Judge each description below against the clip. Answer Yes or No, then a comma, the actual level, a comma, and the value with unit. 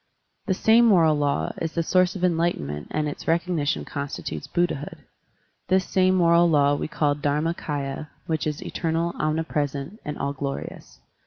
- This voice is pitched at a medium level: Yes, medium, 160 Hz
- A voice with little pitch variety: No, average, 3.2 semitones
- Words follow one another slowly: No, average, 160 wpm